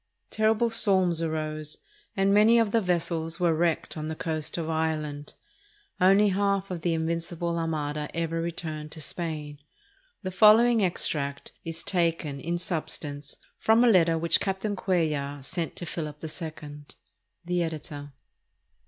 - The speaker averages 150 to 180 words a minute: No, average, 140 wpm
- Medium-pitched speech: Yes, medium, 165 Hz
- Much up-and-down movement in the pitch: No, average, 3.3 semitones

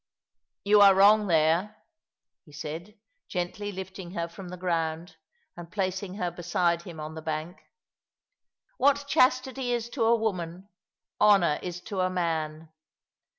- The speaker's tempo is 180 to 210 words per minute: No, average, 145 wpm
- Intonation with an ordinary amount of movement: Yes, average, 3.5 semitones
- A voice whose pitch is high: No, medium, 180 Hz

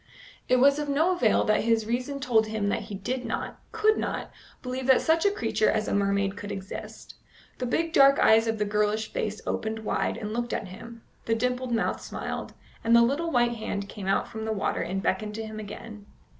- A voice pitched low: No, high, 225 Hz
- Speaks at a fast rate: Yes, fast, 215 wpm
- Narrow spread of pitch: No, average, 3.2 semitones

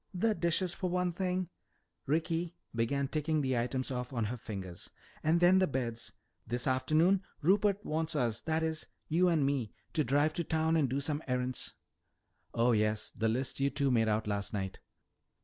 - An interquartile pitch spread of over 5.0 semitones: Yes, wide, 5.4 semitones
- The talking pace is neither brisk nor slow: Yes, average, 180 wpm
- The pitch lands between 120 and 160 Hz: Yes, medium, 140 Hz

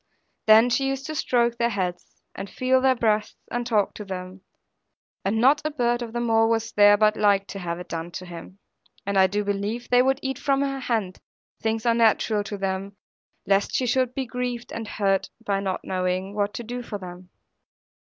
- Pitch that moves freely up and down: No, average, 3.7 semitones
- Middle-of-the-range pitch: No, high, 220 Hz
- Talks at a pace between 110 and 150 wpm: No, average, 200 wpm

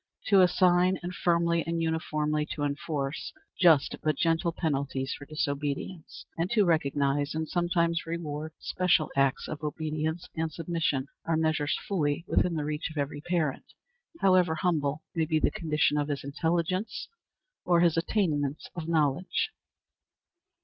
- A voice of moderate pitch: Yes, medium, 160 Hz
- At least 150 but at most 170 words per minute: No, average, 140 wpm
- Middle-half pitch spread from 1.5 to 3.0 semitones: Yes, narrow, 2.6 semitones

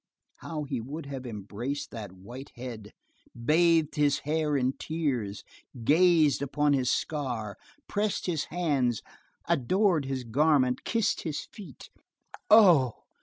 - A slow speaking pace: Yes, slow, 120 wpm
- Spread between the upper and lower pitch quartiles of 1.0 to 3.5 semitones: No, average, 4.6 semitones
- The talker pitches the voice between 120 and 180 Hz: Yes, medium, 140 Hz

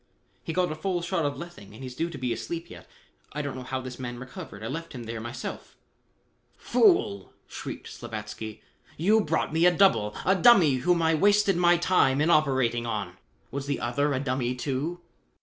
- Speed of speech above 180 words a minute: Yes, average, 195 wpm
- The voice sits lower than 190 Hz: Yes, medium, 140 Hz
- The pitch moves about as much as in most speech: No, wide, 6.1 semitones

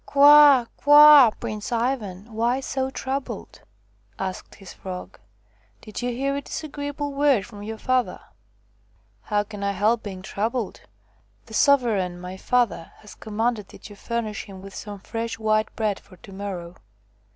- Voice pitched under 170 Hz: No, high, 220 Hz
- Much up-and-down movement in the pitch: No, average, 4.6 semitones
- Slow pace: No, average, 160 wpm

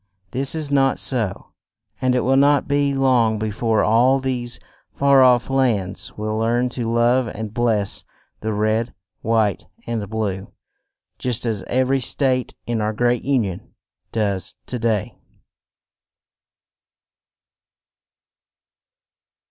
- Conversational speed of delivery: No, slow, 130 wpm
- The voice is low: Yes, low, 120 Hz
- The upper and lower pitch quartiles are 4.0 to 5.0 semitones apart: No, average, 3.1 semitones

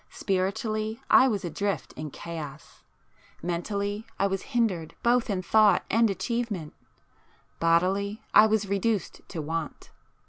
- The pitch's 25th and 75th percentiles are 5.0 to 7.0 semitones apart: No, average, 4.0 semitones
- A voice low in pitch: No, high, 200 Hz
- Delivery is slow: Yes, slow, 110 wpm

